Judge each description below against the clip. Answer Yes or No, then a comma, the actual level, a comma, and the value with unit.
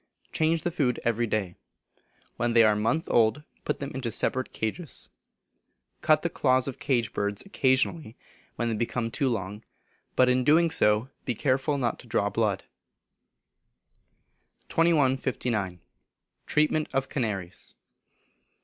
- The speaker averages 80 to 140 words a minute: Yes, slow, 135 wpm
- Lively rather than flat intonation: No, average, 4.5 semitones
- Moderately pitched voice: No, low, 125 Hz